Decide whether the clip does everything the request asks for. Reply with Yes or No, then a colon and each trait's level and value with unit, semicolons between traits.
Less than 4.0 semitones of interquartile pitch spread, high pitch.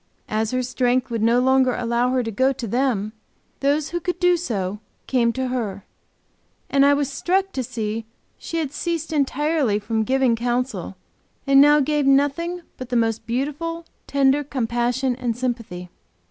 Yes: average, 3.6 semitones; very high, 255 Hz